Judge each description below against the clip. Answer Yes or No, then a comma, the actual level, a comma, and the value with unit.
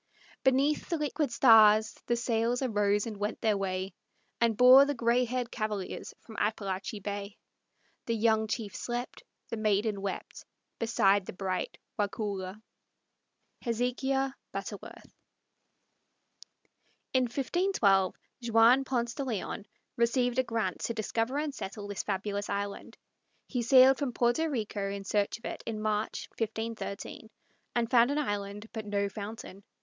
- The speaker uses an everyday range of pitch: Yes, average, 3.4 semitones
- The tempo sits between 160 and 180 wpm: No, slow, 135 wpm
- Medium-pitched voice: No, high, 225 Hz